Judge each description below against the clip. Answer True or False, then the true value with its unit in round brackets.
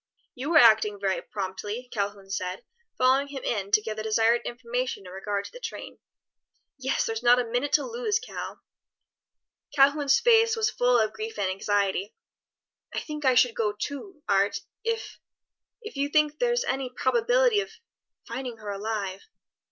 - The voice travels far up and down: True (6.3 semitones)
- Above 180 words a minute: False (165 wpm)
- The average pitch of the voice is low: False (245 Hz)